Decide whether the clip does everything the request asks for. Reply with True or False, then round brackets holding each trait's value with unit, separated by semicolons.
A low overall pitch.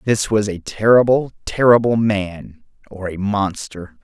True (105 Hz)